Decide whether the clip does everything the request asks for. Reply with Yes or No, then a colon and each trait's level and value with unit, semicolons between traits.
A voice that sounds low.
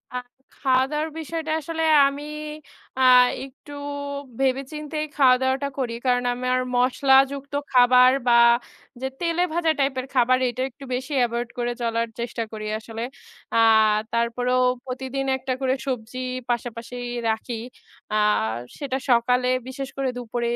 No: very high, 255 Hz